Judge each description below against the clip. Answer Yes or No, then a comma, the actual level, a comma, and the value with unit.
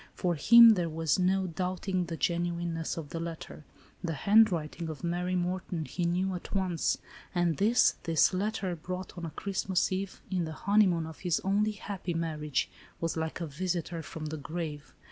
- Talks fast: No, average, 175 wpm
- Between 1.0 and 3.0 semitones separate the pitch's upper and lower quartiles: Yes, narrow, 2.4 semitones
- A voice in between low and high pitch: Yes, medium, 175 Hz